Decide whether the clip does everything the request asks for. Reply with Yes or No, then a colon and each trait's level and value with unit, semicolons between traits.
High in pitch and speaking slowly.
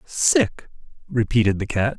No: low, 120 Hz; slow, 120 wpm